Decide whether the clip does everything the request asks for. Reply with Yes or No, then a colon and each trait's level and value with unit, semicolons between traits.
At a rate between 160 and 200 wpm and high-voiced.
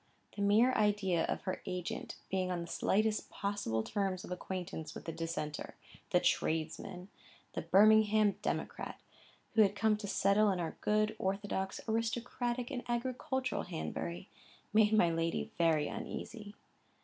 No: average, 140 wpm; high, 200 Hz